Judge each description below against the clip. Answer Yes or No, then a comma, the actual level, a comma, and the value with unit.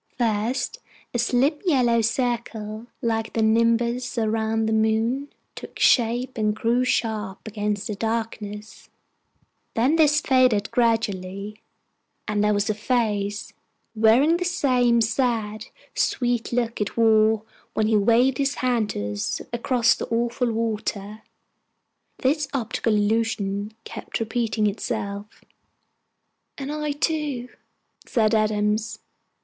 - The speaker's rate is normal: No, slow, 120 wpm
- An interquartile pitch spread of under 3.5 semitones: Yes, narrow, 2.5 semitones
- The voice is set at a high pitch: Yes, high, 225 Hz